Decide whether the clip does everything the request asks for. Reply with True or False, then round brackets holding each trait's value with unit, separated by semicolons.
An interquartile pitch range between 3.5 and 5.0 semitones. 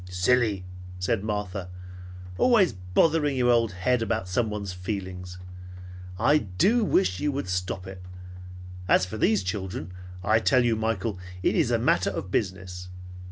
True (4.4 semitones)